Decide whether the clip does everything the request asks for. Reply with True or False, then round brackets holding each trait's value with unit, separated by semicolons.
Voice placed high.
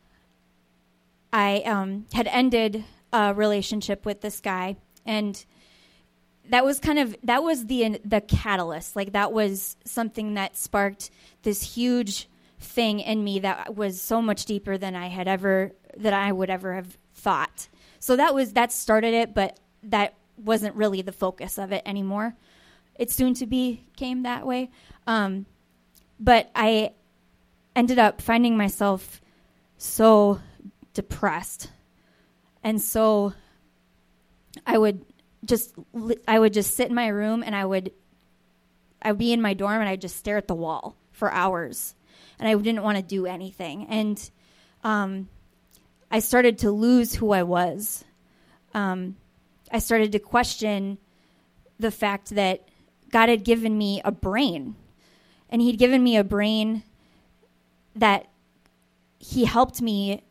True (210 Hz)